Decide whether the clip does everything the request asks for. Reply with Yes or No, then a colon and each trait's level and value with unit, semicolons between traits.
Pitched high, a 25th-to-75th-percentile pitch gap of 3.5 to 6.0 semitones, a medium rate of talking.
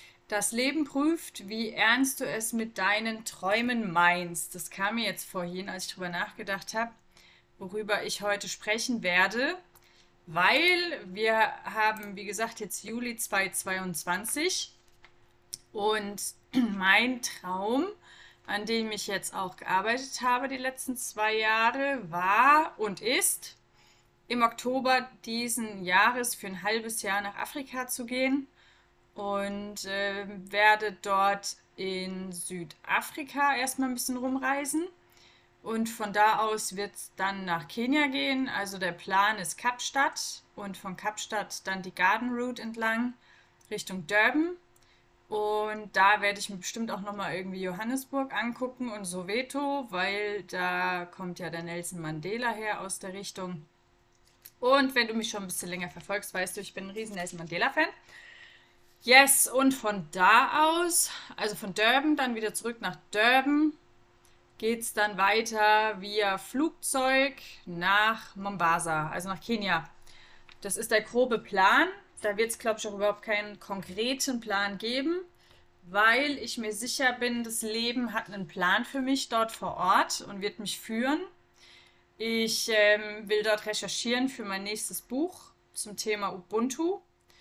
Yes: high, 215 Hz; average, 4.2 semitones; average, 145 wpm